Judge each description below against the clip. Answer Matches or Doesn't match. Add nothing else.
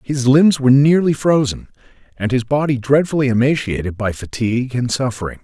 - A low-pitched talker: Matches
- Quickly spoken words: Doesn't match